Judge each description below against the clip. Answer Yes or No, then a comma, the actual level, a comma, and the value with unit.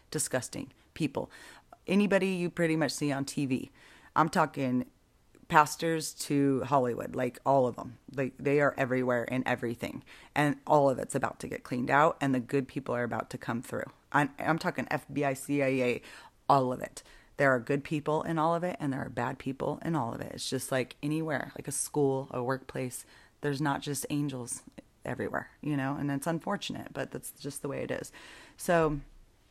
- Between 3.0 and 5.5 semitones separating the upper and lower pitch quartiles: No, narrow, 2.6 semitones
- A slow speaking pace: No, average, 190 wpm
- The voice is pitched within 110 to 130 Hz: No, medium, 140 Hz